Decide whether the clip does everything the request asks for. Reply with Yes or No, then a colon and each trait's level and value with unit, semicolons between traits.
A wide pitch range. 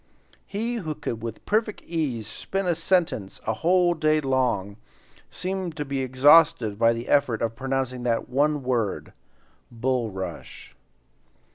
Yes: wide, 6.1 semitones